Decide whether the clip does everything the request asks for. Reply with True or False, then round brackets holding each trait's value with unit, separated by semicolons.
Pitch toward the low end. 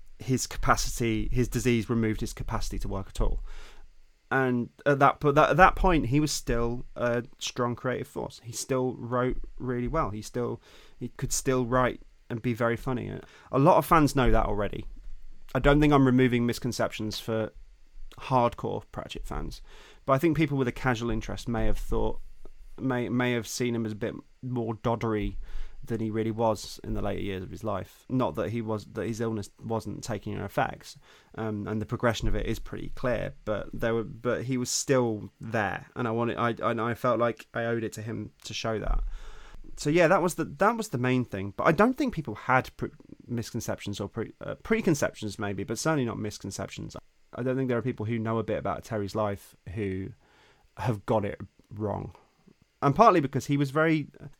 True (120 Hz)